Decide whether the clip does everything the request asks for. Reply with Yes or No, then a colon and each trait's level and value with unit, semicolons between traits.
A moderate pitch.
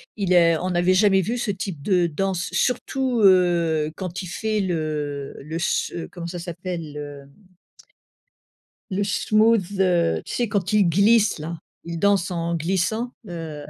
Yes: medium, 180 Hz